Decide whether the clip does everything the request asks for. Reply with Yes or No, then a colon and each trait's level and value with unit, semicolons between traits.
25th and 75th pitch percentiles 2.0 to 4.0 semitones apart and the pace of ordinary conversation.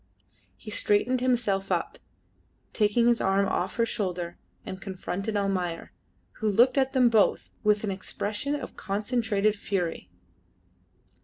No: average, 3.4 semitones; slow, 130 wpm